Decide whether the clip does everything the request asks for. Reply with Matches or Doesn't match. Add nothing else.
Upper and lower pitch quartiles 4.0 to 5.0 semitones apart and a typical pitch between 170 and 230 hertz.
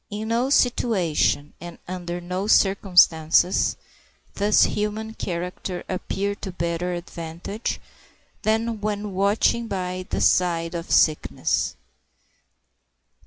Doesn't match